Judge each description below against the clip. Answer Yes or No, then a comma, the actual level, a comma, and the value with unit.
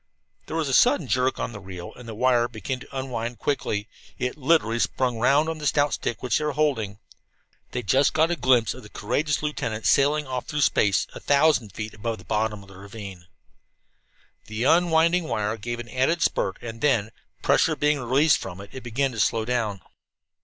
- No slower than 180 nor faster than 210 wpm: Yes, average, 200 wpm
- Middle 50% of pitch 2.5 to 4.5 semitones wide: No, average, 5.0 semitones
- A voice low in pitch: Yes, low, 125 Hz